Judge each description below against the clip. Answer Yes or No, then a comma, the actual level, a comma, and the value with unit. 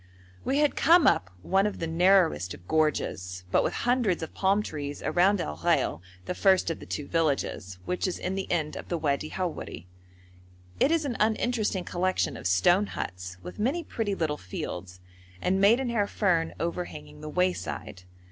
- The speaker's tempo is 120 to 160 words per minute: No, average, 175 wpm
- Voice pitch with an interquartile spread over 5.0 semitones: Yes, wide, 5.5 semitones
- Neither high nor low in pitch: Yes, medium, 180 Hz